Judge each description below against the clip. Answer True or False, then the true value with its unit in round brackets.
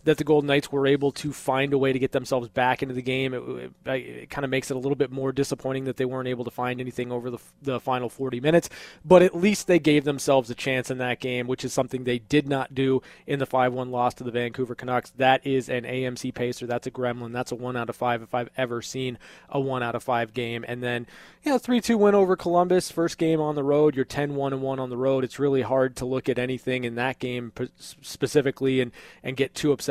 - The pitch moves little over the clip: True (2.0 semitones)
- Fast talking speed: True (255 wpm)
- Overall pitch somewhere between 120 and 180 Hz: True (130 Hz)